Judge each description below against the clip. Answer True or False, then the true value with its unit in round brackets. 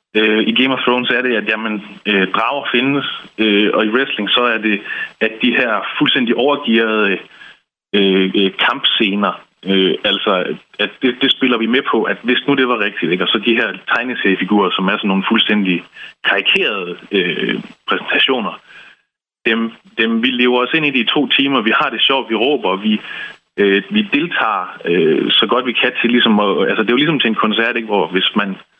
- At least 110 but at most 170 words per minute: False (200 wpm)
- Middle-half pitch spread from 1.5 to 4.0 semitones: True (3.3 semitones)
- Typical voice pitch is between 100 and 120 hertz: True (110 Hz)